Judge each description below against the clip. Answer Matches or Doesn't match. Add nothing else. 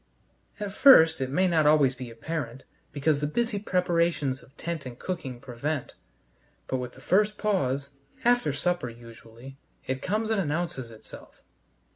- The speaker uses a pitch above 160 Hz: Doesn't match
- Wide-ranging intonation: Matches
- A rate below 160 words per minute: Matches